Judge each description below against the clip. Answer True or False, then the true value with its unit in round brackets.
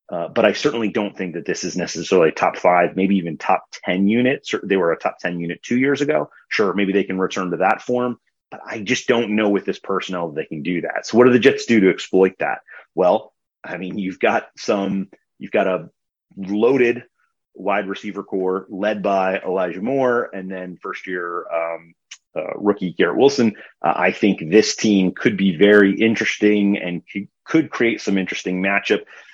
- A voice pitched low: True (100 Hz)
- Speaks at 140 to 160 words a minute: False (200 wpm)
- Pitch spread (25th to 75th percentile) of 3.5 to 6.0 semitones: False (2.8 semitones)